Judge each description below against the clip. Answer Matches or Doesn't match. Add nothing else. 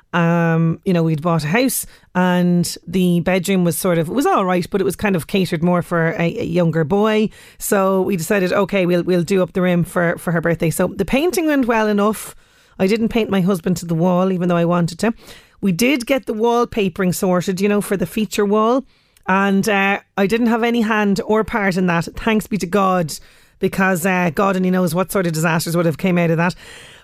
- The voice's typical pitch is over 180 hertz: Matches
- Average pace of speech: Doesn't match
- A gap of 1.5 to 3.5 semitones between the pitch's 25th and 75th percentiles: Matches